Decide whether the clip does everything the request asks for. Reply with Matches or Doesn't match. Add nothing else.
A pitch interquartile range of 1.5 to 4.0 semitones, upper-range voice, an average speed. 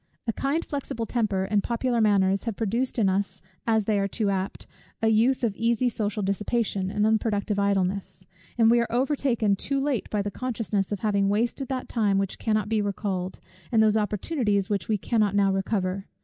Matches